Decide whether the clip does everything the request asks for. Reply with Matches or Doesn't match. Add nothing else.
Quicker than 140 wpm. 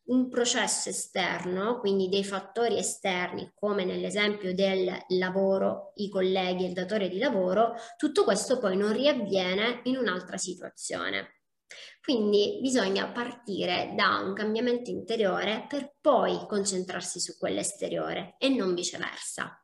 Doesn't match